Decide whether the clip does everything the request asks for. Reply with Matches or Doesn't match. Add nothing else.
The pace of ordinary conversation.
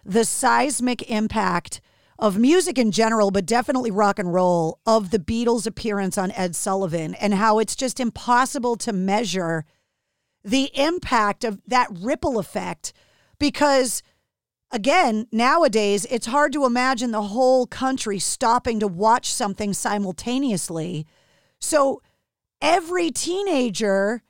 Doesn't match